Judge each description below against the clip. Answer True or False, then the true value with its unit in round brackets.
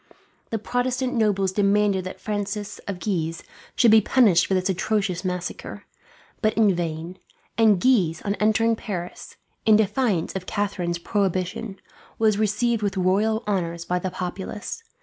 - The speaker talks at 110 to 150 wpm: True (145 wpm)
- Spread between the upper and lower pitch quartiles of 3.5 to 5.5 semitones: False (3.1 semitones)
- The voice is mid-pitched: False (200 Hz)